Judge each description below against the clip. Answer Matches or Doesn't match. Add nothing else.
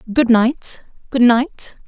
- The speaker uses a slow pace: Matches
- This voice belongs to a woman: Matches